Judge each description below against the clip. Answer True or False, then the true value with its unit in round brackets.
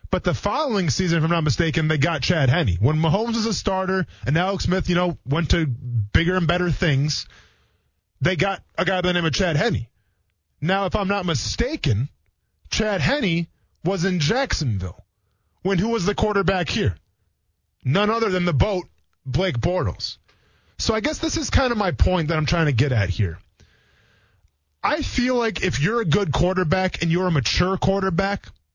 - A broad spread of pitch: True (8.3 semitones)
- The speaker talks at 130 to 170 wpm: False (190 wpm)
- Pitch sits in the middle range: True (165 Hz)